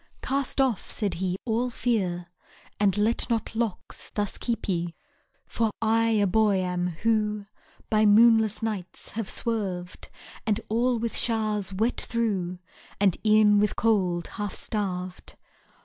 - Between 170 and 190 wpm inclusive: No, slow, 135 wpm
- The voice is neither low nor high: No, high, 210 Hz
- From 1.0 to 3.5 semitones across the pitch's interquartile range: Yes, average, 3.1 semitones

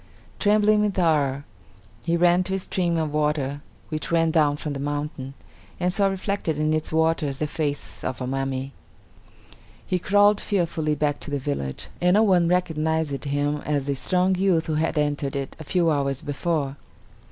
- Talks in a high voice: No, medium, 155 Hz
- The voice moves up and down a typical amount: Yes, average, 3.7 semitones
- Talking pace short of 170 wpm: No, average, 175 wpm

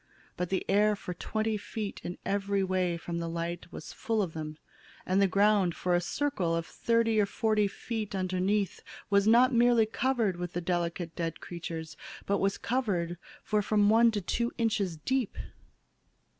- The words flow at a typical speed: Yes, average, 170 wpm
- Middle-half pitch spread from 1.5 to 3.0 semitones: No, average, 3.9 semitones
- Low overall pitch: No, high, 200 Hz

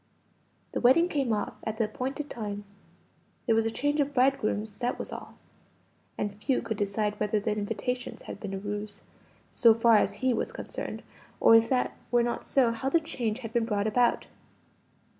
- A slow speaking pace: No, average, 185 wpm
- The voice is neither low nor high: No, high, 225 Hz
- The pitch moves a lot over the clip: No, average, 3.1 semitones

